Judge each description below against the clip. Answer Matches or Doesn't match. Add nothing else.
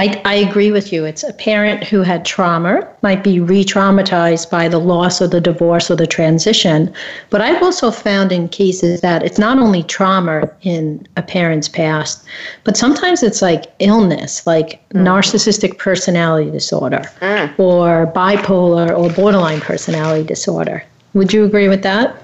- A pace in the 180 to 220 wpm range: Doesn't match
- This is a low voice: Doesn't match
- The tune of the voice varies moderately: Matches